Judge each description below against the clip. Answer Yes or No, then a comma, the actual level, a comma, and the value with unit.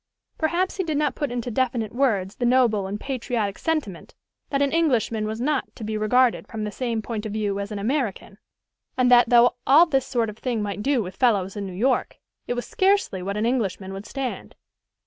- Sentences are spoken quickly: Yes, fast, 210 wpm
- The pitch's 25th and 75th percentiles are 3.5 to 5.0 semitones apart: Yes, average, 4.2 semitones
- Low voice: No, high, 235 Hz